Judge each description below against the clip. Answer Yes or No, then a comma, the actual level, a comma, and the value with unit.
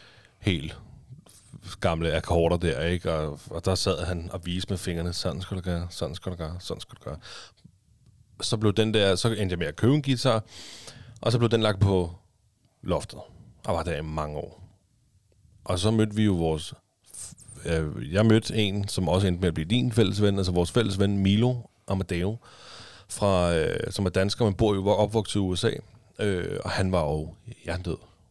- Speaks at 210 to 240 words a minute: No, average, 195 wpm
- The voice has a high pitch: No, very low, 95 Hz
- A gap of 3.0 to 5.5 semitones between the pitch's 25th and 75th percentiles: Yes, average, 3.8 semitones